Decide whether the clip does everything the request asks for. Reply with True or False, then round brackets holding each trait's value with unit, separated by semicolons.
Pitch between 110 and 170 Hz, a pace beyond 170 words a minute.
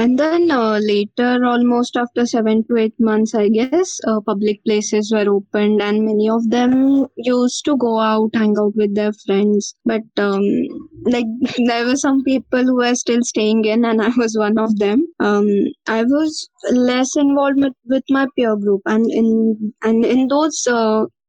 False (230 Hz; 180 wpm)